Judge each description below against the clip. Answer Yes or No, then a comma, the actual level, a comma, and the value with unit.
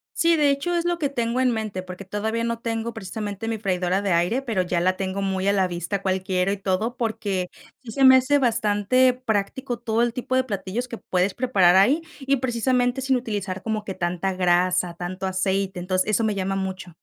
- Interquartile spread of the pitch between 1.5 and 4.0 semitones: No, average, 4.6 semitones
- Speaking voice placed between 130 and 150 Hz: No, high, 205 Hz